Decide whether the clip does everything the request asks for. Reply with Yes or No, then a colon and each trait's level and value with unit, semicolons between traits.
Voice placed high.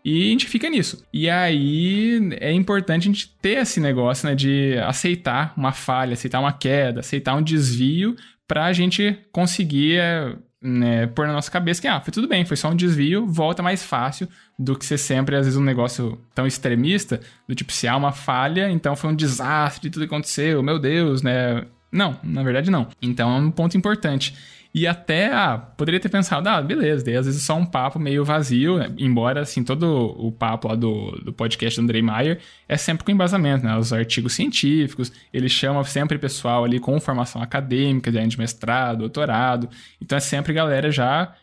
No: medium, 140 Hz